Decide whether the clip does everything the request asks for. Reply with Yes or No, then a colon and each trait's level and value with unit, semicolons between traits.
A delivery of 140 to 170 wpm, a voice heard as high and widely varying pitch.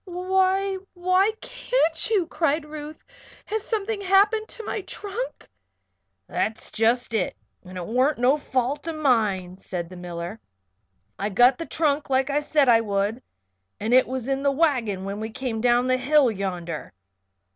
Yes: average, 160 wpm; very high, 265 Hz; wide, 8.1 semitones